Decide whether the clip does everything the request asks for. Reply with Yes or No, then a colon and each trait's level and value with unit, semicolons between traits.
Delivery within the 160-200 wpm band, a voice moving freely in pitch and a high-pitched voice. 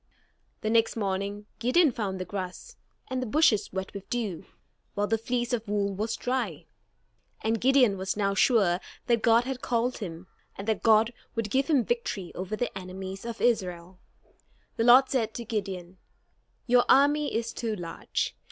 No: average, 170 wpm; average, 3.9 semitones; high, 220 Hz